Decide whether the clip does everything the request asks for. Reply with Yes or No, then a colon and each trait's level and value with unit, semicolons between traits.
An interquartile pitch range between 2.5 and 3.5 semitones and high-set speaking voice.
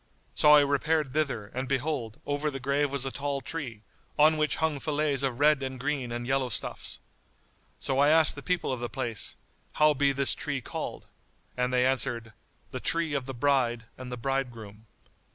No: average, 2.9 semitones; low, 135 Hz